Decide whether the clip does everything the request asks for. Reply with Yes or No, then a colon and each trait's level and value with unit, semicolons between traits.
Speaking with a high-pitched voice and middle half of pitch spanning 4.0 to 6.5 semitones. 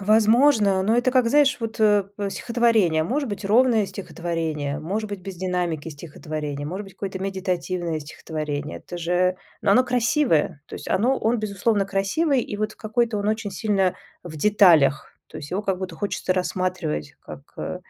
Yes: high, 195 Hz; average, 4.3 semitones